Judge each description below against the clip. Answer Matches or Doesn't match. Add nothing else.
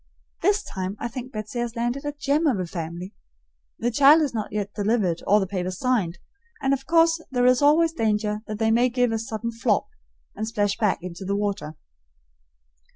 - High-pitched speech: Matches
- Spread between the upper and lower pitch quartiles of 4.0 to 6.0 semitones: Matches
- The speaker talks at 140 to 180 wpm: Doesn't match